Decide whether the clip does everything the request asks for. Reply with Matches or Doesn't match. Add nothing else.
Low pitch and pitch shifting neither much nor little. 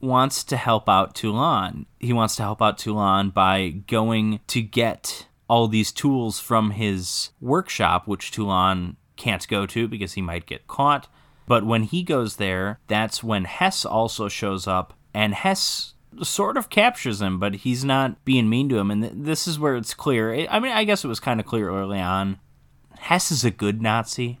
Matches